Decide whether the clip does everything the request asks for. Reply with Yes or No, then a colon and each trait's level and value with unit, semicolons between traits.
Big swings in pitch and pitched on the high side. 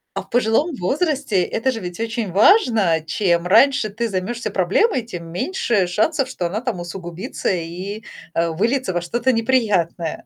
Yes: wide, 5.7 semitones; high, 215 Hz